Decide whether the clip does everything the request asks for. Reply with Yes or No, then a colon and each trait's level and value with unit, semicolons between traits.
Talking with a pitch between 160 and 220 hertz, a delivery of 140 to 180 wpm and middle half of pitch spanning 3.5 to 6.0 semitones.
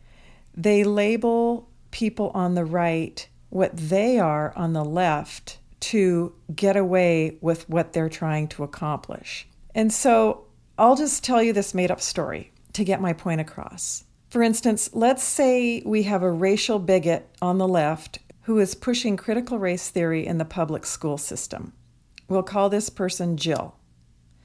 Yes: medium, 185 Hz; average, 155 wpm; average, 4.8 semitones